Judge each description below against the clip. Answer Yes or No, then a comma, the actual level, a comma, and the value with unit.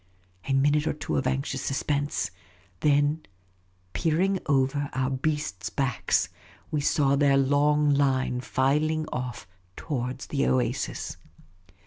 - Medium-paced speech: No, slow, 120 wpm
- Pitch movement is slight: Yes, narrow, 2.0 semitones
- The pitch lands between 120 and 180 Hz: Yes, medium, 140 Hz